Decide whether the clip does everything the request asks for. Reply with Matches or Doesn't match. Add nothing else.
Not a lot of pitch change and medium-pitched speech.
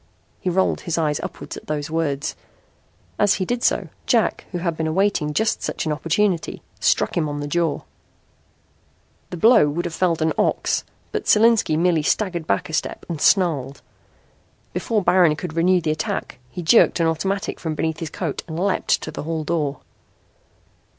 Doesn't match